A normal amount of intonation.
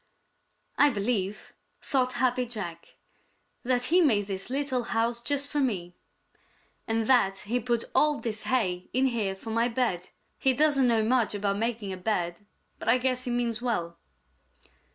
Yes: average, 3.8 semitones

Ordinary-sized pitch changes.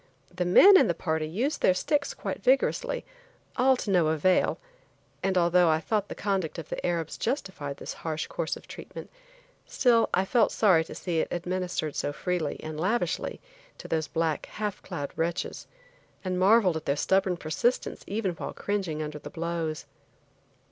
Yes: average, 4.1 semitones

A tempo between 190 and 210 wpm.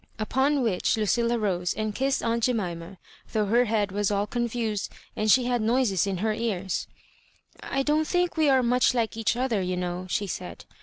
Yes: average, 195 wpm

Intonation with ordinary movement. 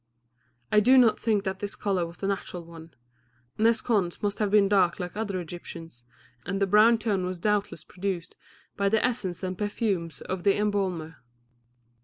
Yes: average, 3.0 semitones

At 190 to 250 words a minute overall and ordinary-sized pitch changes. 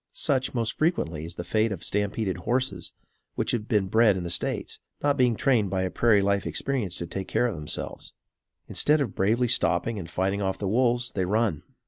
Yes: average, 200 wpm; average, 4.3 semitones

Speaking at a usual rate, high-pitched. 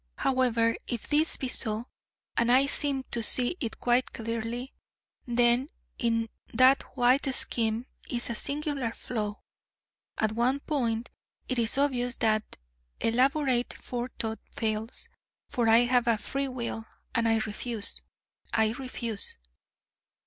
No: slow, 125 wpm; high, 240 Hz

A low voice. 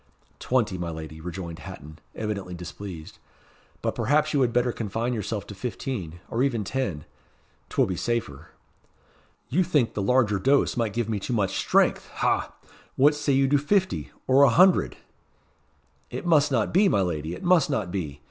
Yes: low, 115 Hz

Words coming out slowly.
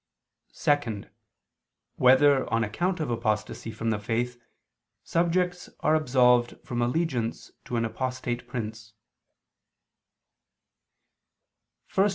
Yes: slow, 90 wpm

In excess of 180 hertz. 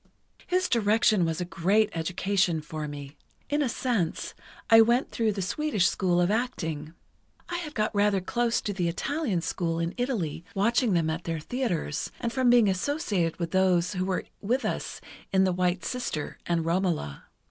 Yes: high, 190 Hz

